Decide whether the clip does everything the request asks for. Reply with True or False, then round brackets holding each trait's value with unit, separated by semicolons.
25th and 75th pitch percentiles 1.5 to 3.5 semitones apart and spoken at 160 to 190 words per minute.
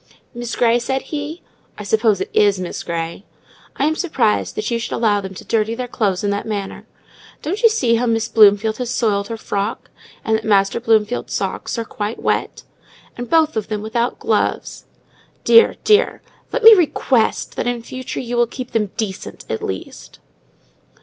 True (3.2 semitones; 185 wpm)